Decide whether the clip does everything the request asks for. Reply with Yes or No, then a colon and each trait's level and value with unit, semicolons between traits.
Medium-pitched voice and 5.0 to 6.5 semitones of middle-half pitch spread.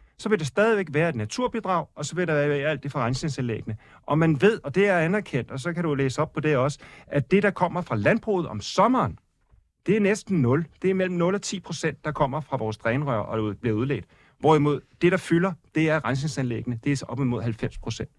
Yes: medium, 150 Hz; wide, 5.6 semitones